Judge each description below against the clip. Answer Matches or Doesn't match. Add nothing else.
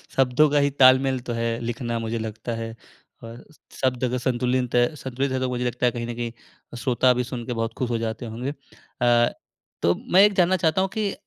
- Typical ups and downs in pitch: Doesn't match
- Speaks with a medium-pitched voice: Doesn't match